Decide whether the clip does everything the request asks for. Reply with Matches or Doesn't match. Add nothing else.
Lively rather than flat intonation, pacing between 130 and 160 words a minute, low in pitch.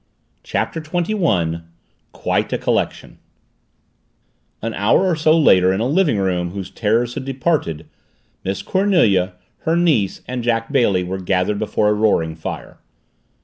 Matches